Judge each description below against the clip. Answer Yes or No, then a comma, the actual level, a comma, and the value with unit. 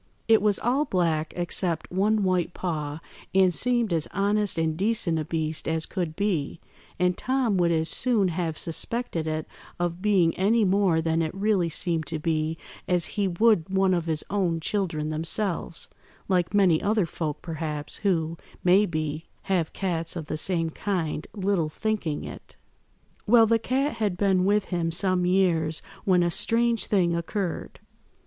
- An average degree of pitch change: Yes, average, 3.8 semitones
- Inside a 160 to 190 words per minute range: Yes, average, 165 wpm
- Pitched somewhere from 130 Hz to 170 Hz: No, medium, 180 Hz